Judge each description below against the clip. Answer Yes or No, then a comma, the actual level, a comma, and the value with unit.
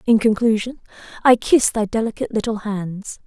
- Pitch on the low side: No, high, 220 Hz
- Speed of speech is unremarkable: Yes, average, 145 wpm